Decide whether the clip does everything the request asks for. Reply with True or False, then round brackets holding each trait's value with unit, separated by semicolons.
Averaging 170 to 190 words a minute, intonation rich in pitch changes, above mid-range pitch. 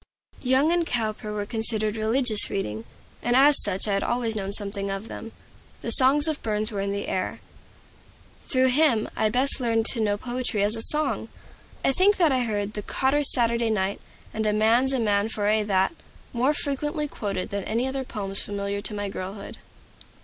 False (185 wpm; 4.1 semitones; 220 Hz)